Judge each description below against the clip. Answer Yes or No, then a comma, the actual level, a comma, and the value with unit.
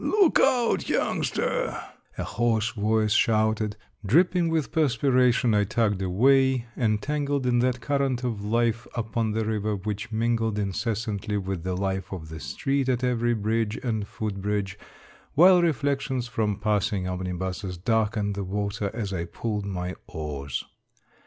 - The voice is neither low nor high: No, low, 110 Hz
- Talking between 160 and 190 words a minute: No, average, 140 wpm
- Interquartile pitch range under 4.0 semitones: Yes, average, 3.5 semitones